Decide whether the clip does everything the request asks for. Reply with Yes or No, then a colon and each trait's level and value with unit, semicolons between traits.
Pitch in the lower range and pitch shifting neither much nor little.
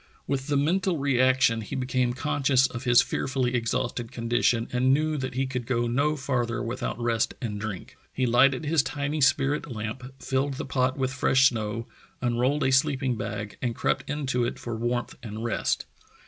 No: low, 130 Hz; narrow, 2.3 semitones